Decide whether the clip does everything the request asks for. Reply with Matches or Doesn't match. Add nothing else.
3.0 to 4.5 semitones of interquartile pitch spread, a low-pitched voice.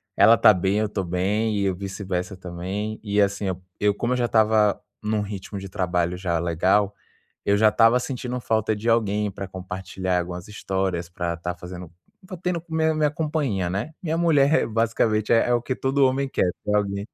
Matches